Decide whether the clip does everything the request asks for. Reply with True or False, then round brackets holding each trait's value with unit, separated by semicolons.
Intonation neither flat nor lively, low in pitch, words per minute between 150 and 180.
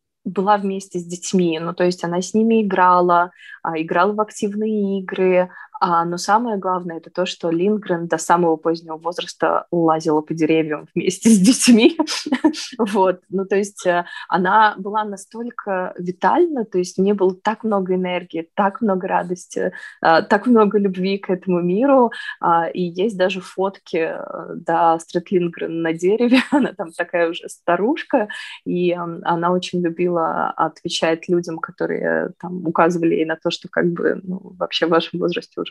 False (3.3 semitones; 180 Hz; 155 wpm)